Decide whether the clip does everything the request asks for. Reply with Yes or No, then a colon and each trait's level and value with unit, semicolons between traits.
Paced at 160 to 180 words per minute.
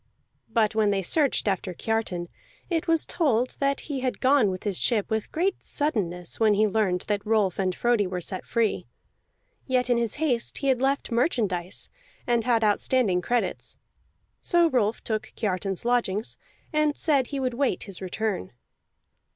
Yes: average, 165 wpm